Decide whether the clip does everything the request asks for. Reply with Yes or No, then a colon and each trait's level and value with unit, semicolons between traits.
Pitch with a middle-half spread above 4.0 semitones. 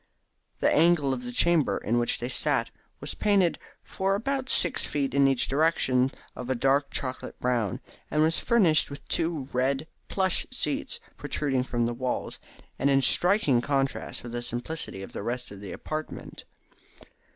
Yes: average, 4.7 semitones